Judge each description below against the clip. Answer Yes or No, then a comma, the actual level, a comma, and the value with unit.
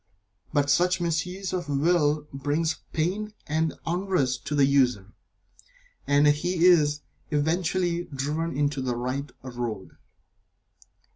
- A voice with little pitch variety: No, average, 3.7 semitones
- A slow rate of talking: Yes, slow, 120 wpm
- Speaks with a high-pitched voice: No, medium, 150 Hz